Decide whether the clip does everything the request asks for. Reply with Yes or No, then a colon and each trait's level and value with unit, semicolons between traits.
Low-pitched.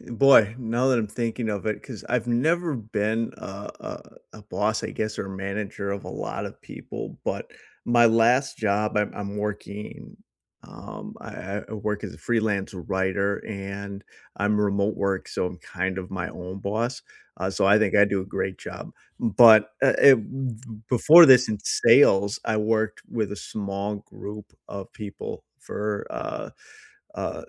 Yes: low, 105 Hz